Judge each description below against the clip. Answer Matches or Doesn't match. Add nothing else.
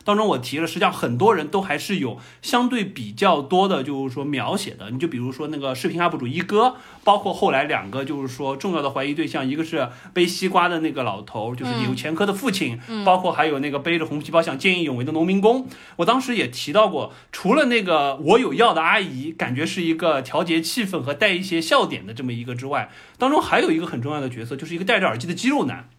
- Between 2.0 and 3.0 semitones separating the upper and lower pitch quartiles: Doesn't match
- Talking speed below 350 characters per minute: Doesn't match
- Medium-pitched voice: Matches